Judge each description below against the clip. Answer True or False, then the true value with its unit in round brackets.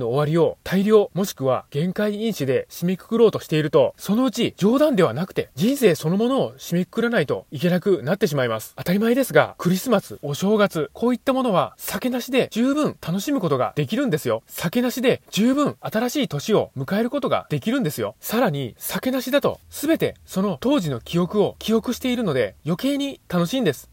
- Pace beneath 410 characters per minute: False (415 characters per minute)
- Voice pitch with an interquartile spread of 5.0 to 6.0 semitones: False (6.7 semitones)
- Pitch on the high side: True (210 Hz)